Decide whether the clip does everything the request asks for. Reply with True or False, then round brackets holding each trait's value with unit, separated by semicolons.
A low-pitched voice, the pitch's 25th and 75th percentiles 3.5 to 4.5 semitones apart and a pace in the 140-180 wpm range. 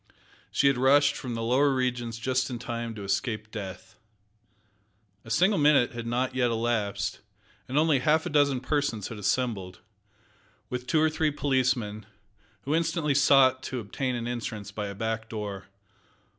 True (125 Hz; 3.8 semitones; 160 wpm)